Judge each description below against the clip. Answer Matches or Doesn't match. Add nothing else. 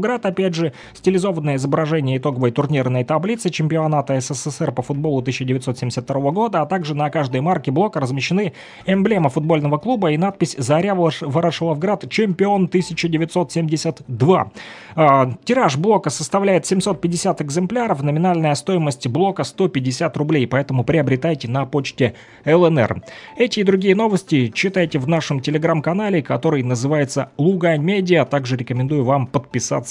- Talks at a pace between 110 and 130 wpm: Matches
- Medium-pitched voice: Matches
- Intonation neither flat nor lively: Matches